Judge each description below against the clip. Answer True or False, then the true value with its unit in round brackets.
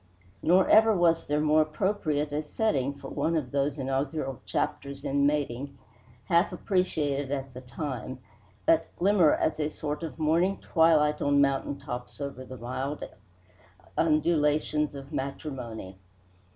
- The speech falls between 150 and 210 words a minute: False (140 wpm)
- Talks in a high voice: False (145 Hz)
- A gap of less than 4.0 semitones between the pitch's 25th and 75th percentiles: True (2.8 semitones)